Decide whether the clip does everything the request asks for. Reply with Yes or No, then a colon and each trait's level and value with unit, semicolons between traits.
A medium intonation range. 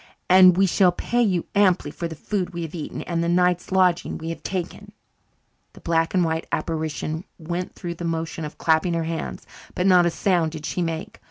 No: narrow, 1.9 semitones